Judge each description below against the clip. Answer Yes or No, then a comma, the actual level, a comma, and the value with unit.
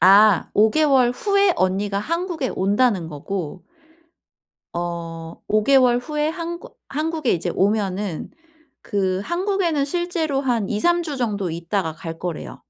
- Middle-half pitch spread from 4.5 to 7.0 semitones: No, wide, 8.9 semitones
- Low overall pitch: No, high, 215 Hz